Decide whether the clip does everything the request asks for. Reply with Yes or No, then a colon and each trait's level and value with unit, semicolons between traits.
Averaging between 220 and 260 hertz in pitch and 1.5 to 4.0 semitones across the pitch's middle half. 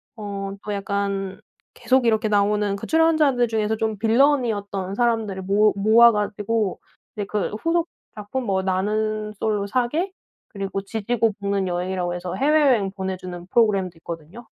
No: high, 210 Hz; average, 2.9 semitones